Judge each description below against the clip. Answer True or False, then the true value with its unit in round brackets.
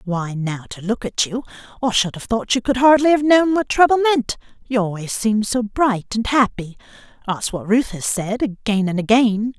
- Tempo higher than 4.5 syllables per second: True (4.9 syllables/s)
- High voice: True (225 Hz)